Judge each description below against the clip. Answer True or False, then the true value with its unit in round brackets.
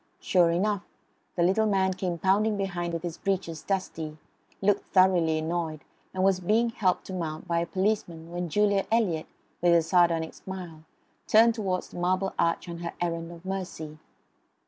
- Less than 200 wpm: True (170 wpm)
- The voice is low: False (180 Hz)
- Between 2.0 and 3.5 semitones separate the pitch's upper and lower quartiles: True (2.5 semitones)